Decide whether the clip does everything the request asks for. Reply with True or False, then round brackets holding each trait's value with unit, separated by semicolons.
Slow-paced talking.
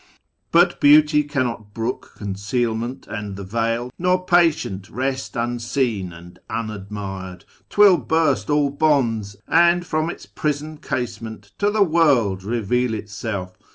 True (120 wpm)